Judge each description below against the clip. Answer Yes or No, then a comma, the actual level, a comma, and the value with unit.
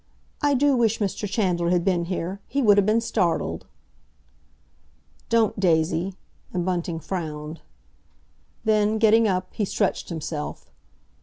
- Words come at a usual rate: No, slow, 130 wpm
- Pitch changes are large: No, average, 4.2 semitones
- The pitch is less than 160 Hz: No, high, 190 Hz